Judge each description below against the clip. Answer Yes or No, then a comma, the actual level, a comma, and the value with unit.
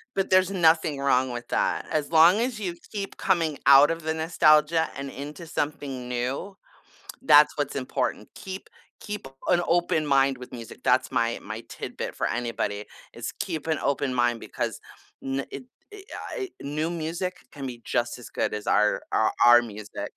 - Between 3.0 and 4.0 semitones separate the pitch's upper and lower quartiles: No, average, 5.3 semitones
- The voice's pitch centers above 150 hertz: No, medium, 145 Hz